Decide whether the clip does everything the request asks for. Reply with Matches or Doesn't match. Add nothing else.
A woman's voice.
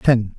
Doesn't match